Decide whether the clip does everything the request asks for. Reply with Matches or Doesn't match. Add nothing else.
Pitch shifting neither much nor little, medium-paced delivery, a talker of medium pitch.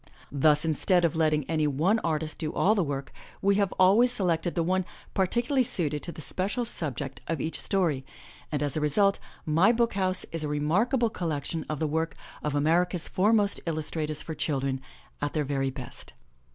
Matches